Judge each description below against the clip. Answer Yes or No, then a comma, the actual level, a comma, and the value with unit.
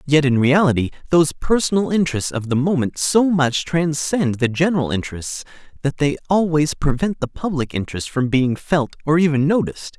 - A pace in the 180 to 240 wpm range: No, average, 170 wpm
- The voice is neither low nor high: Yes, medium, 150 Hz